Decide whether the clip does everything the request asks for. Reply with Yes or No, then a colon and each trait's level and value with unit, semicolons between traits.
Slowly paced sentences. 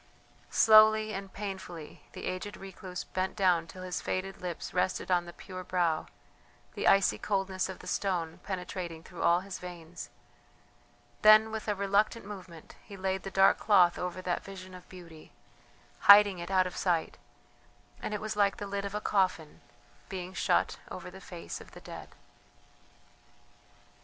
No: average, 160 wpm